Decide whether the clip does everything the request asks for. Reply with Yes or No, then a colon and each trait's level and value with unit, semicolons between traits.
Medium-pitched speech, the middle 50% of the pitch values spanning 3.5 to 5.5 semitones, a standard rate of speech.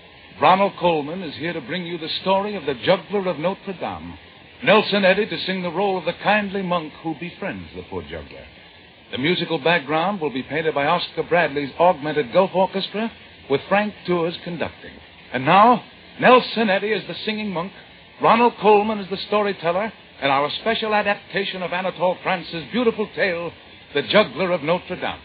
Yes: medium, 180 Hz; average, 4.1 semitones; average, 175 wpm